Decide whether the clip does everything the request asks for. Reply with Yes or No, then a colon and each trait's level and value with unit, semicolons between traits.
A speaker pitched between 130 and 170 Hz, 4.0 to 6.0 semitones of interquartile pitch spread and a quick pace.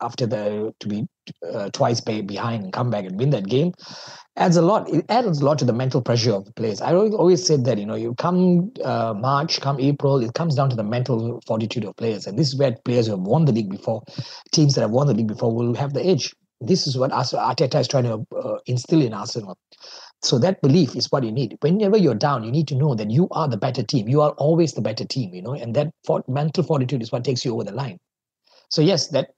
Yes: low, 135 Hz; average, 4.9 semitones; fast, 255 wpm